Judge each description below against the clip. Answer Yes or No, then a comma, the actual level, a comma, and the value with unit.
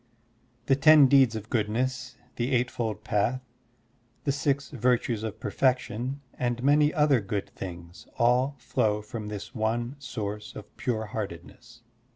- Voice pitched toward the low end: Yes, low, 120 Hz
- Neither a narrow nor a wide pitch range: Yes, average, 3.5 semitones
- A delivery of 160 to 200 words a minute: No, slow, 135 wpm